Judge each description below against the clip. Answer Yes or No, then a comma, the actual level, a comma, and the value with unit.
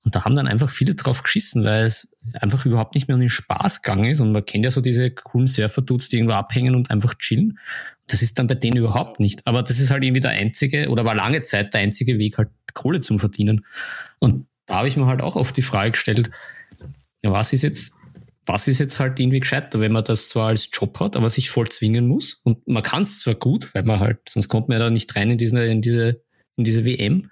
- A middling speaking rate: No, fast, 250 wpm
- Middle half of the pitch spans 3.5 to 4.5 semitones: No, average, 3.0 semitones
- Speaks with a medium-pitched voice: No, low, 120 Hz